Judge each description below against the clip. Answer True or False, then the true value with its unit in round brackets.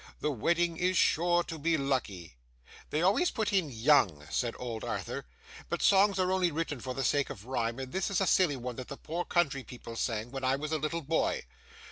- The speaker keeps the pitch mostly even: False (5.6 semitones)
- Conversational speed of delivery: False (215 wpm)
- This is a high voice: False (145 Hz)